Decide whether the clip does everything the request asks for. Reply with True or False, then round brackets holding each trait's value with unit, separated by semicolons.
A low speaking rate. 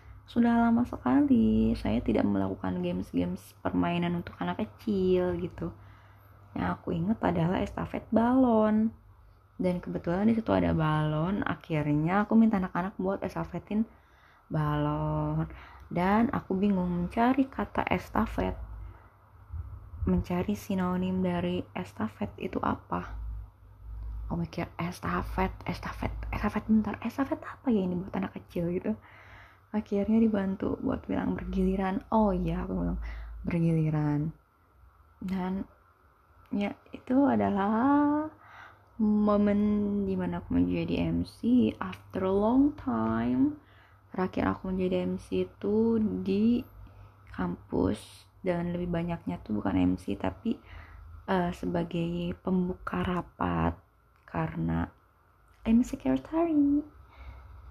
False (105 wpm)